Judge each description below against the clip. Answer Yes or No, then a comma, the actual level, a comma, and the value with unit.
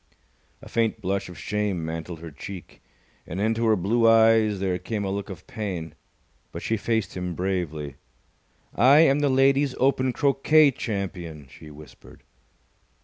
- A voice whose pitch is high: No, low, 100 Hz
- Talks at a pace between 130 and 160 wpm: Yes, average, 150 wpm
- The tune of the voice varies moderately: Yes, average, 4.7 semitones